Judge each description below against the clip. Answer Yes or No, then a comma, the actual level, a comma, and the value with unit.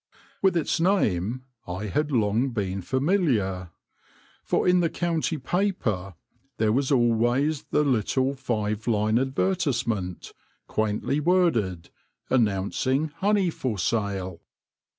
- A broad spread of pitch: Yes, wide, 6.6 semitones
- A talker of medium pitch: No, low, 120 Hz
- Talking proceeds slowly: Yes, slow, 110 wpm